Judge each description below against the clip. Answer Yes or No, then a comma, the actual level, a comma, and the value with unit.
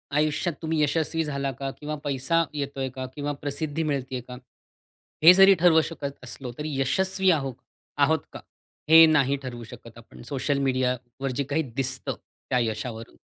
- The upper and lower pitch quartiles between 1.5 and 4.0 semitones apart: Yes, average, 3.4 semitones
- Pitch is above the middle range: No, medium, 140 Hz